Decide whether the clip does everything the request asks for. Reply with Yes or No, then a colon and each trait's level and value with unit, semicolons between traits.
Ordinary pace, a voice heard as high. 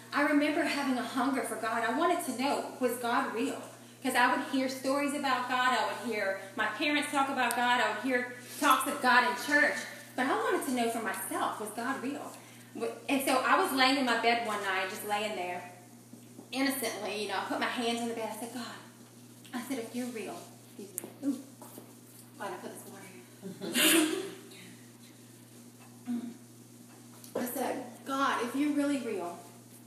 Yes: average, 180 wpm; very high, 250 Hz